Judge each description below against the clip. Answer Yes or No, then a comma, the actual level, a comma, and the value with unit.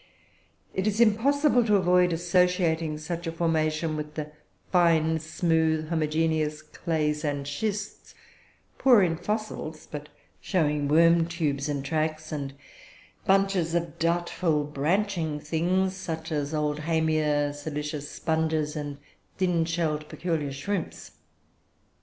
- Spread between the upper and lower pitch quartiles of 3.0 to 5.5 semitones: No, narrow, 2.6 semitones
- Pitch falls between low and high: Yes, medium, 160 Hz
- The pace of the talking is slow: Yes, slow, 115 wpm